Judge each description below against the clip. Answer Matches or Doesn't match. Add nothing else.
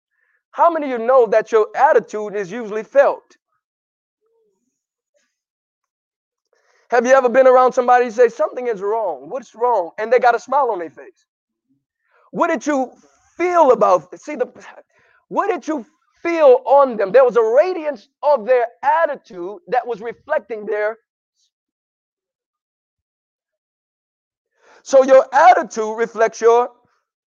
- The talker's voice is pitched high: Matches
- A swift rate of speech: Doesn't match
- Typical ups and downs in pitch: Doesn't match